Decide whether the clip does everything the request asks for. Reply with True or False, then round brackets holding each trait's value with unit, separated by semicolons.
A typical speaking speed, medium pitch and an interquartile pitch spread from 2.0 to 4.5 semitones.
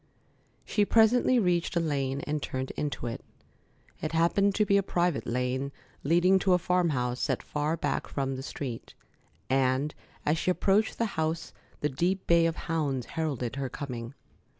False (170 wpm; 155 Hz; 5.1 semitones)